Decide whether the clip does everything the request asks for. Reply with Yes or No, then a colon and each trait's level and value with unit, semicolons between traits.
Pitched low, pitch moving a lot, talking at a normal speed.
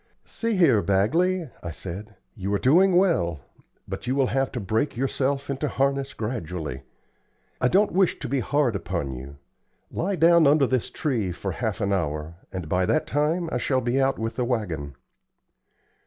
Yes: low, 125 Hz; wide, 7.5 semitones; average, 175 wpm